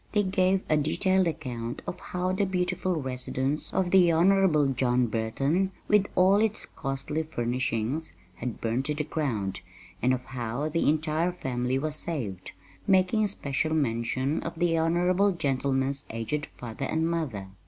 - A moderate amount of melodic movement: No, wide, 5.9 semitones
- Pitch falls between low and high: Yes, medium, 150 Hz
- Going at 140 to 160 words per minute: Yes, average, 150 wpm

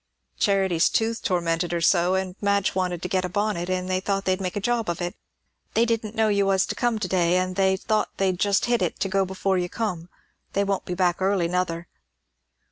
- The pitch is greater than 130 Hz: Yes, high, 190 Hz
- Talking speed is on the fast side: Yes, fast, 220 wpm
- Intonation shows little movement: Yes, narrow, 2.1 semitones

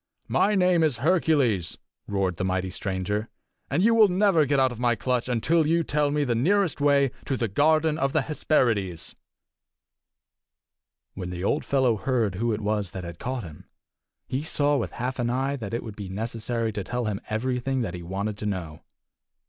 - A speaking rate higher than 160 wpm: Yes, average, 190 wpm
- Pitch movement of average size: No, wide, 6.1 semitones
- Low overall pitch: Yes, low, 120 Hz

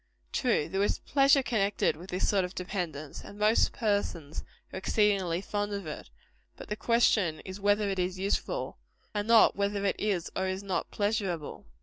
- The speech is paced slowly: No, average, 180 wpm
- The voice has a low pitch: No, high, 200 Hz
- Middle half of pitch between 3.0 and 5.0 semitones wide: No, narrow, 2.4 semitones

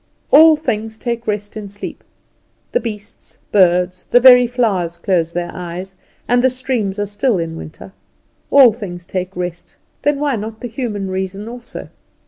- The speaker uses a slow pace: No, average, 160 wpm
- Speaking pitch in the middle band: No, high, 205 Hz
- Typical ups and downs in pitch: Yes, average, 5.0 semitones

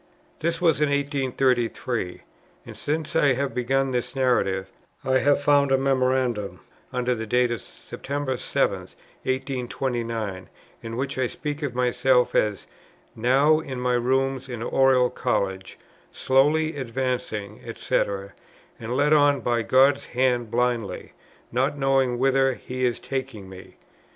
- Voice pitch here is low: Yes, low, 130 Hz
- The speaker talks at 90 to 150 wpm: Yes, slow, 135 wpm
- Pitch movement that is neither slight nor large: No, narrow, 2.1 semitones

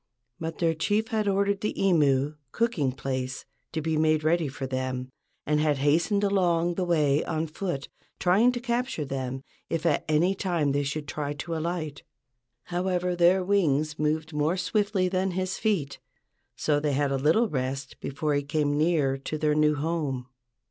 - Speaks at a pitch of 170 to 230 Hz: No, medium, 155 Hz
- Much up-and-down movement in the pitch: No, average, 4.1 semitones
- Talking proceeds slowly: No, average, 170 wpm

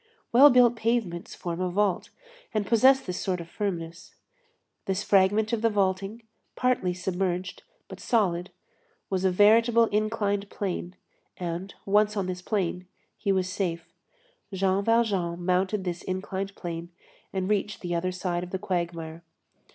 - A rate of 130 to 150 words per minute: Yes, average, 145 wpm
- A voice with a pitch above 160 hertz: Yes, high, 190 Hz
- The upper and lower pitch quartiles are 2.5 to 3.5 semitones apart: Yes, average, 2.8 semitones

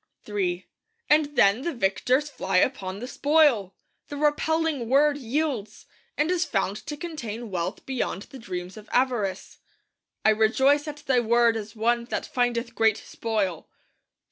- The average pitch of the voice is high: Yes, high, 240 Hz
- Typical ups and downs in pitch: No, wide, 5.7 semitones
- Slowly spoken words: No, average, 145 wpm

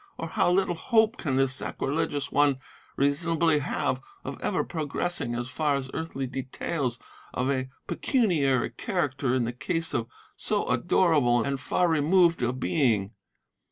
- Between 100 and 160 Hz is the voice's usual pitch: Yes, medium, 140 Hz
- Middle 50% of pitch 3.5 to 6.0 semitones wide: Yes, average, 4.4 semitones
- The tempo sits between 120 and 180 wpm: Yes, average, 145 wpm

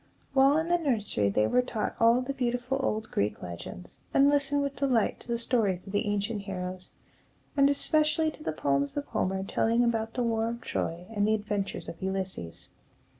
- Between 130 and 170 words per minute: No, average, 190 wpm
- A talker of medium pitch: No, high, 225 Hz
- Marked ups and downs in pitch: Yes, wide, 5.8 semitones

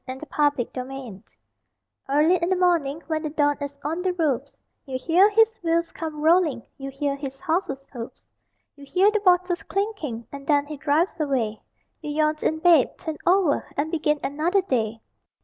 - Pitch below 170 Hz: No, very high, 305 Hz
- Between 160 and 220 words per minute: Yes, average, 175 wpm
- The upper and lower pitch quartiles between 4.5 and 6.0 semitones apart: No, average, 4.0 semitones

